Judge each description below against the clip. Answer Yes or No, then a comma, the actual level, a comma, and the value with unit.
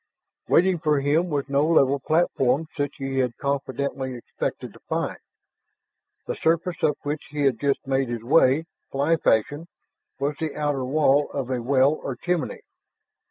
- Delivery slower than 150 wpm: No, average, 160 wpm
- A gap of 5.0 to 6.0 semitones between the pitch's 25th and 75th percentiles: No, narrow, 2.6 semitones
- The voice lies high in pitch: No, medium, 140 Hz